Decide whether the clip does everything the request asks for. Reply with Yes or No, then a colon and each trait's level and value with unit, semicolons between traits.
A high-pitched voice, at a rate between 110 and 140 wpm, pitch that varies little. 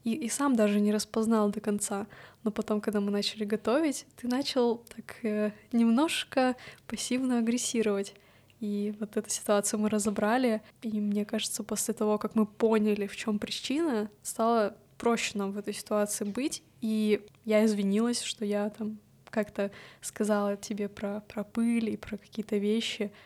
No: high, 215 Hz; average, 155 wpm; narrow, 1.7 semitones